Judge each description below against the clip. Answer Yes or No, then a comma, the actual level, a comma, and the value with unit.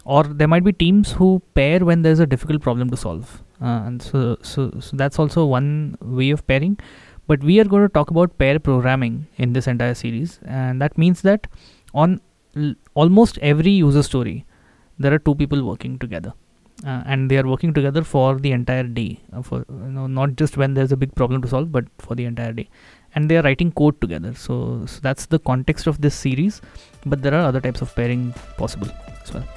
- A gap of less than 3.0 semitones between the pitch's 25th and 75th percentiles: No, average, 3.7 semitones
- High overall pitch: No, low, 135 Hz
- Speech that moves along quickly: Yes, fast, 215 wpm